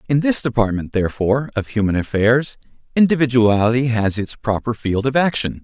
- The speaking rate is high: No, average, 150 wpm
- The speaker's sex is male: Yes, male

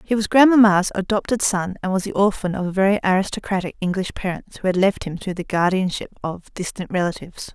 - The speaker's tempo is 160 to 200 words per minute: Yes, average, 190 wpm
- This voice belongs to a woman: Yes, female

